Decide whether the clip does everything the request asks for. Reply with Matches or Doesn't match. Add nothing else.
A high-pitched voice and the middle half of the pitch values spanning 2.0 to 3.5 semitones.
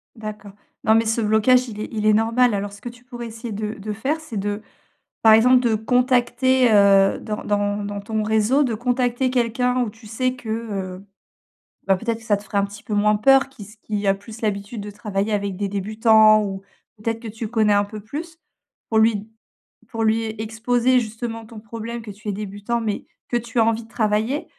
Matches